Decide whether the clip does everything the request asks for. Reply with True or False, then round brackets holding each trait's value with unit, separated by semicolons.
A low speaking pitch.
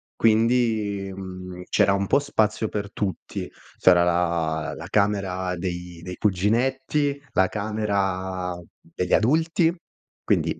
True (100 Hz)